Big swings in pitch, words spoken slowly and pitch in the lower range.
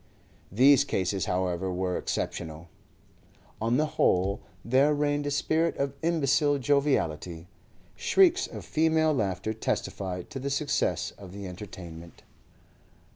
Yes: wide, 8.0 semitones; slow, 120 wpm; low, 115 Hz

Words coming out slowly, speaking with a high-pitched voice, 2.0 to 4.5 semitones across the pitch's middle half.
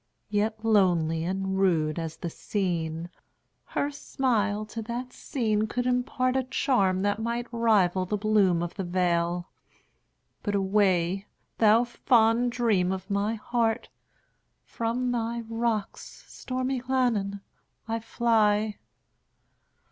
Yes: slow, 105 wpm; high, 215 Hz; average, 3.8 semitones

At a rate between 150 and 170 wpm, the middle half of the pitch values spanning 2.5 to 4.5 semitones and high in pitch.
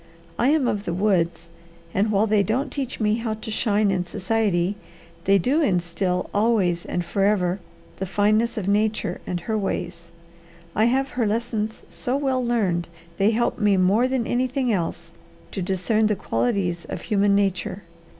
Yes: average, 165 wpm; average, 3.7 semitones; high, 205 Hz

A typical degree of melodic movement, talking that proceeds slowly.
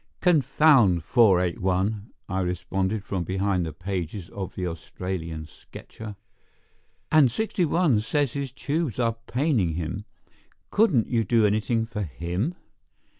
No: wide, 5.7 semitones; slow, 120 wpm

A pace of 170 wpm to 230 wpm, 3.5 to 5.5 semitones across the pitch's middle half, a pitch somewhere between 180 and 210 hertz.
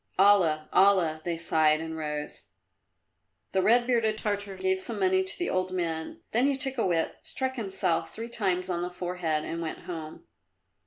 Yes: average, 175 wpm; average, 3.9 semitones; medium, 185 Hz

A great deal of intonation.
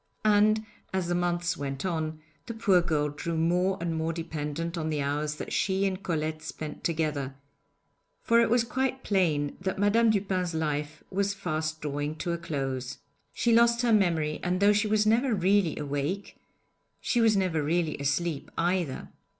No: average, 4.6 semitones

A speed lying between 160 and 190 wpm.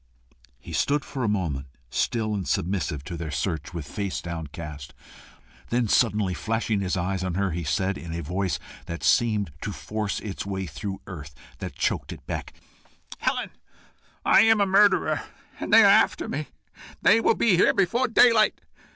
Yes: average, 170 wpm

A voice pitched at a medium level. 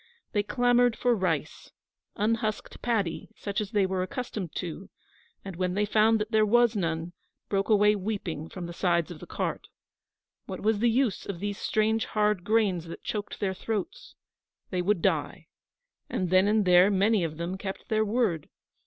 No: high, 205 Hz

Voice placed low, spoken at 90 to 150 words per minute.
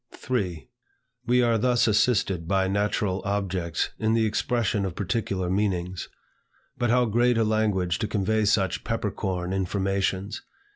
Yes: low, 100 Hz; average, 140 wpm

